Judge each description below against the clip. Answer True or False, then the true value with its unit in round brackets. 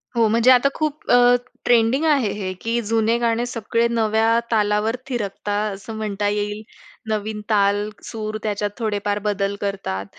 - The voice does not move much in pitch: True (2.1 semitones)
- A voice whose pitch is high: True (215 Hz)